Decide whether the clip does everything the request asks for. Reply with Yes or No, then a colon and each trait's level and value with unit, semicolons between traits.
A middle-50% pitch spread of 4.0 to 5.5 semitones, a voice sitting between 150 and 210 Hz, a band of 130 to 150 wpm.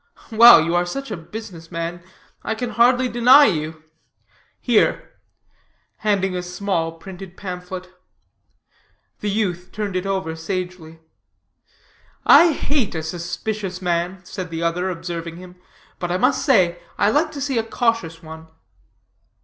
Yes: average, 4.3 semitones; medium, 185 Hz; average, 140 wpm